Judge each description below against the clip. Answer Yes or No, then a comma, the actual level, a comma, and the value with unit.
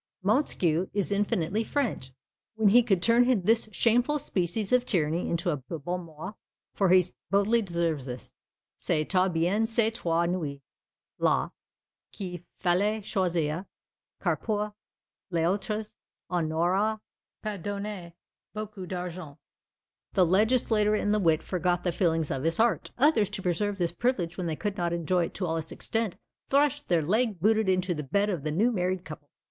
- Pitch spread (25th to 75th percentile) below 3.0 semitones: No, average, 4.1 semitones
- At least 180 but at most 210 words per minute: No, average, 165 wpm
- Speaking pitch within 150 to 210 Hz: Yes, medium, 185 Hz